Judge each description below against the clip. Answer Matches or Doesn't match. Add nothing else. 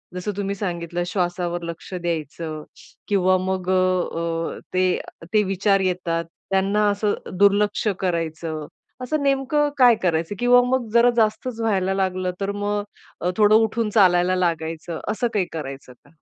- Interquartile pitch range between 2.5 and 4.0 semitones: Matches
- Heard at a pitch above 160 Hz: Matches